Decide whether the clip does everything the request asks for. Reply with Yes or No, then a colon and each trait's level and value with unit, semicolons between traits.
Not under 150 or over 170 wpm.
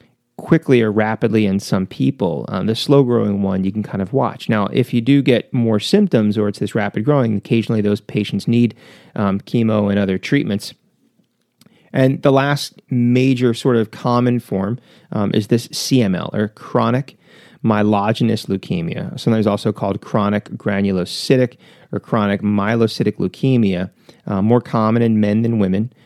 Yes: average, 160 wpm